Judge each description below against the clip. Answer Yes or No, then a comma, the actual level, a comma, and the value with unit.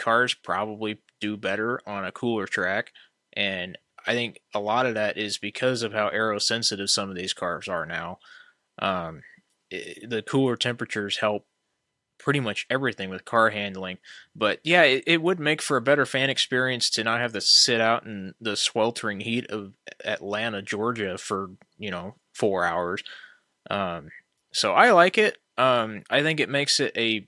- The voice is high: No, low, 115 Hz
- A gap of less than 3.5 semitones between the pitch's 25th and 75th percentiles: No, average, 4.0 semitones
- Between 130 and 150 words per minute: No, average, 175 wpm